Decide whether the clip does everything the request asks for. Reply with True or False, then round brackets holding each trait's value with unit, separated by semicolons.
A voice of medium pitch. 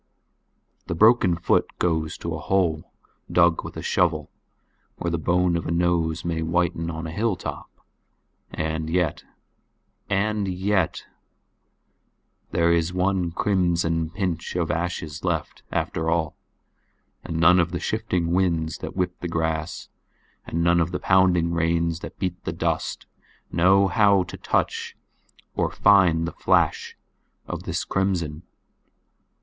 False (85 Hz)